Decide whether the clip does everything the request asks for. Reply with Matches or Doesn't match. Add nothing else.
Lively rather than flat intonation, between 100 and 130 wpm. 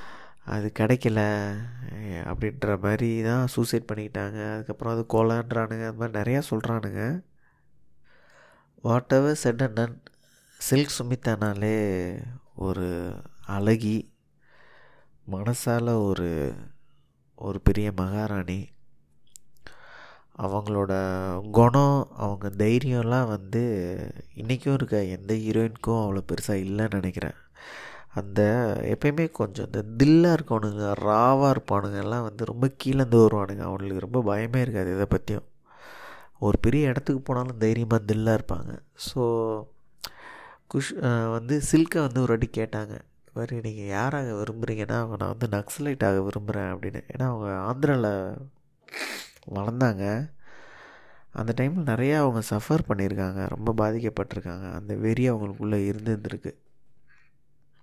Doesn't match